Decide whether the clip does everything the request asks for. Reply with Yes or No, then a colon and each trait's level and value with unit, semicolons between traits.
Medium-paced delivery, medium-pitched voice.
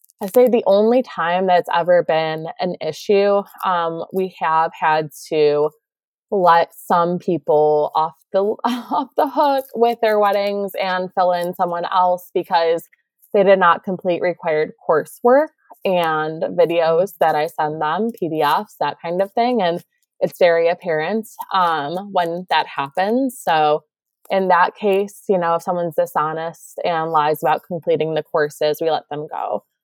Yes: average, 155 wpm; medium, 175 Hz